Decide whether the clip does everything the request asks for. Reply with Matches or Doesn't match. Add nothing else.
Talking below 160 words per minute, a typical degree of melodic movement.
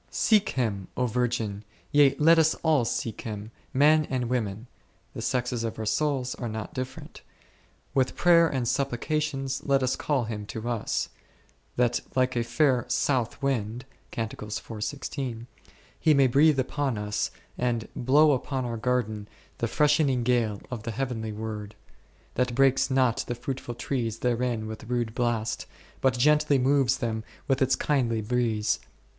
Matches